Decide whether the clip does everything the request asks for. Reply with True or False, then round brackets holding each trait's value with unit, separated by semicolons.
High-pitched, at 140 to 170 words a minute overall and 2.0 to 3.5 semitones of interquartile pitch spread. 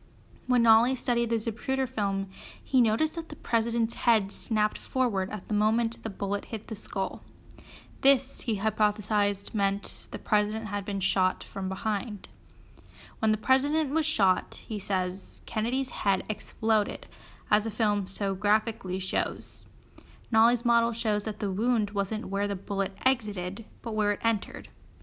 True (220 Hz; 155 wpm; 2.5 semitones)